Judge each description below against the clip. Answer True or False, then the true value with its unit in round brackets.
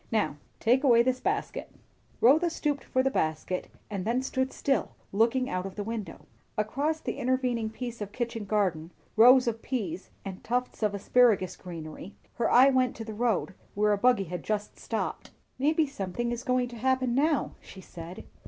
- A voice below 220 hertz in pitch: False (235 Hz)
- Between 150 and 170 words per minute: False (180 wpm)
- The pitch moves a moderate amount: True (4.2 semitones)